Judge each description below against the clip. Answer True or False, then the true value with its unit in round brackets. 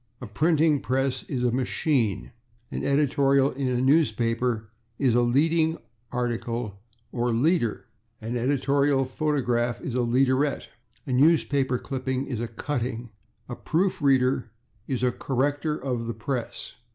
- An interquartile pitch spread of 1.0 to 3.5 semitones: True (2.9 semitones)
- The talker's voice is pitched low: True (130 Hz)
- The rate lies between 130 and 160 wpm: True (135 wpm)